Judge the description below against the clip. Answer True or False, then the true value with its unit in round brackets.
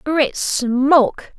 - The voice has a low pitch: False (270 Hz)